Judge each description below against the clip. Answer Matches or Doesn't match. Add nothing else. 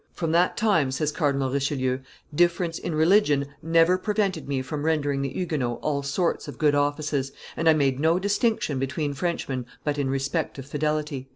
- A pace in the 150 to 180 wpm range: Matches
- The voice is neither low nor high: Matches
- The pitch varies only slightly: Doesn't match